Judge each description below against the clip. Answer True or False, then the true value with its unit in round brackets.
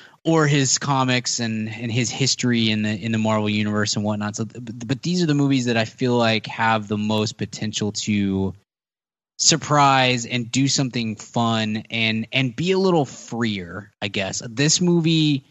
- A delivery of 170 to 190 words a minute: True (180 wpm)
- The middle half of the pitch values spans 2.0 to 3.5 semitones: False (4.0 semitones)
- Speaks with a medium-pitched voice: False (115 Hz)